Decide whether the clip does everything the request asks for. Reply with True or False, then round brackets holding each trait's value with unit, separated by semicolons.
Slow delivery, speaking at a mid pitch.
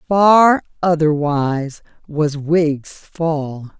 True (80 wpm; 155 Hz)